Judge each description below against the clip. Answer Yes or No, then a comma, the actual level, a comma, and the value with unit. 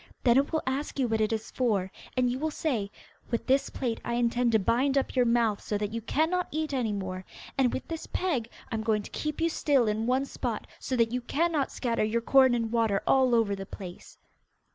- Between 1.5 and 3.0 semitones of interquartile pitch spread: No, average, 3.6 semitones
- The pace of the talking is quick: Yes, fast, 230 wpm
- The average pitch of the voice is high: Yes, high, 240 Hz